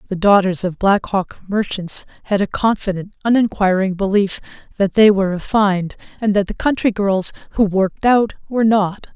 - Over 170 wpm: No, average, 165 wpm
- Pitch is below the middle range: No, high, 200 Hz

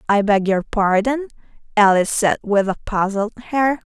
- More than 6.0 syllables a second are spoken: No, 5.0 syllables/s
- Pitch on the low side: No, high, 215 Hz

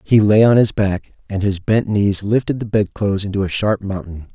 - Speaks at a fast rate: Yes, fast, 235 wpm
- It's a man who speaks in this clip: Yes, male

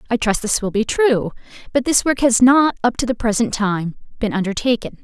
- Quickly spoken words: Yes, fast, 215 wpm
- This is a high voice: Yes, high, 230 Hz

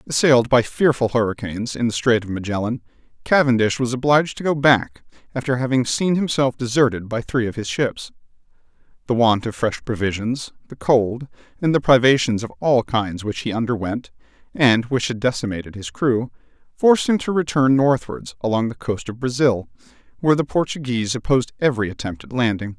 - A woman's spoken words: No, male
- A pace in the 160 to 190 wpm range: Yes, average, 170 wpm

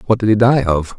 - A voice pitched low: Yes, low, 105 Hz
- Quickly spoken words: Yes, fast, 305 wpm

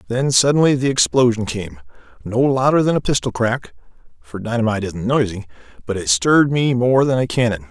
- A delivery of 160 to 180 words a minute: Yes, average, 170 wpm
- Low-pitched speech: Yes, low, 120 Hz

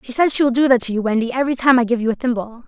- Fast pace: Yes, fast, 360 wpm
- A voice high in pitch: Yes, high, 245 Hz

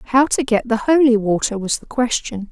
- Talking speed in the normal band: No, fast, 215 wpm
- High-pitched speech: Yes, high, 235 Hz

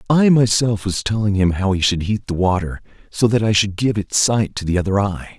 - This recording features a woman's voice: No, male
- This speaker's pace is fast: Yes, fast, 245 wpm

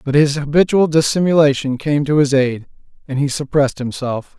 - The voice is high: No, medium, 145 Hz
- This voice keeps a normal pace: Yes, average, 165 wpm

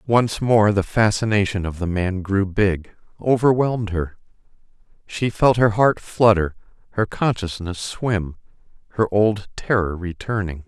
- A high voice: No, low, 100 Hz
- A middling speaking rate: No, slow, 130 wpm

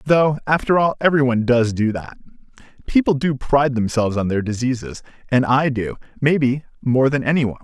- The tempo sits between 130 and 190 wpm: Yes, average, 175 wpm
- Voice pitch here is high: No, low, 130 Hz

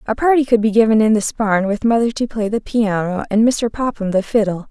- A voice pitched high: Yes, high, 220 Hz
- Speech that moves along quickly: Yes, fast, 240 wpm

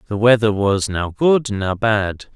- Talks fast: No, average, 180 wpm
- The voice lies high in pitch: No, low, 105 Hz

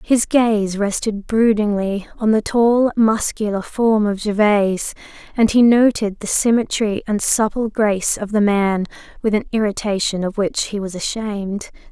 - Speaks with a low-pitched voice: No, high, 210 Hz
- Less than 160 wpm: Yes, average, 150 wpm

